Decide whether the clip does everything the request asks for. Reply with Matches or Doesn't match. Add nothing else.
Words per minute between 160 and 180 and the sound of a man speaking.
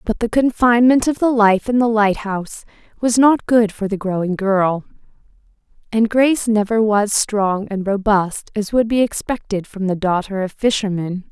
Doesn't match